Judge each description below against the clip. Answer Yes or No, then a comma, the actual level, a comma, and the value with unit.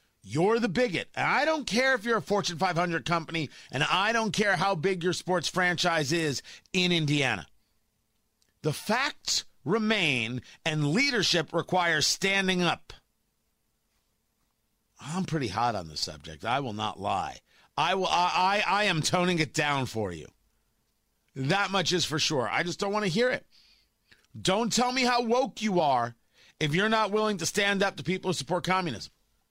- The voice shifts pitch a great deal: Yes, wide, 6.9 semitones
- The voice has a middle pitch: Yes, medium, 175 Hz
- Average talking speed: Yes, average, 175 wpm